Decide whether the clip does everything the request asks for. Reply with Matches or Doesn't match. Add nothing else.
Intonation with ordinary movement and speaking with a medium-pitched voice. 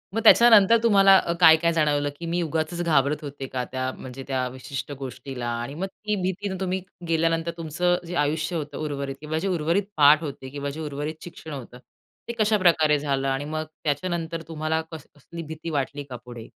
Matches